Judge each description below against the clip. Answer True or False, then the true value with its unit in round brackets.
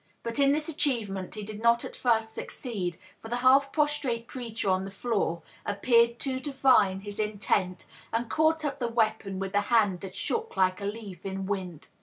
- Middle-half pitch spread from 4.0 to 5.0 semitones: True (4.7 semitones)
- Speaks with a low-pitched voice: False (225 Hz)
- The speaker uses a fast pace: False (190 wpm)